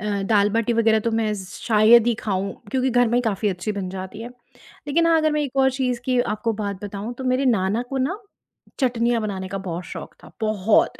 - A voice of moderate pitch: No, high, 225 Hz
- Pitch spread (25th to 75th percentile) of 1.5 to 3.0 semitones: No, average, 3.4 semitones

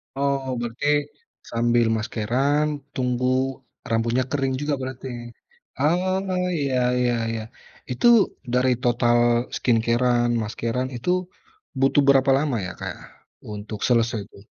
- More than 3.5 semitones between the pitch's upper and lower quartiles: No, average, 2.8 semitones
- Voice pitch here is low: Yes, low, 125 Hz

